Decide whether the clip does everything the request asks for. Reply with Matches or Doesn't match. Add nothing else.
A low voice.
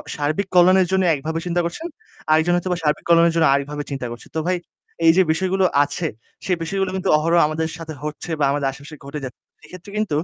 Doesn't match